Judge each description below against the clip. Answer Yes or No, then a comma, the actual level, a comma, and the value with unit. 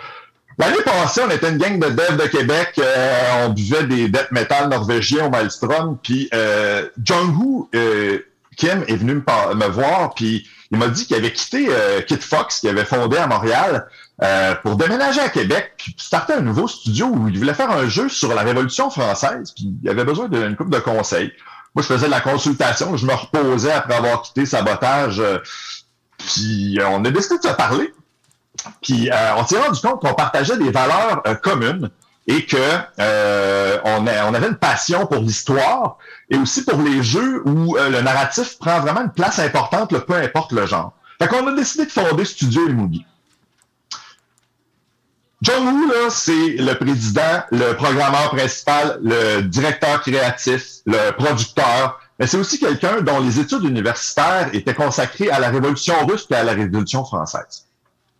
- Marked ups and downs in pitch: Yes, wide, 5.7 semitones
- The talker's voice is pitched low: Yes, low, 130 Hz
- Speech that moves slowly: No, average, 185 wpm